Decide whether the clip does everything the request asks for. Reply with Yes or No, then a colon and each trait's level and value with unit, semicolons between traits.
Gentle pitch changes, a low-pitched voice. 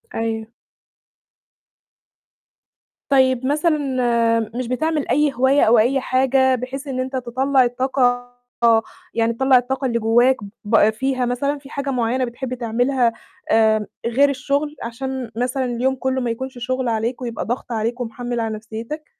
No: narrow, 2.2 semitones; very high, 255 Hz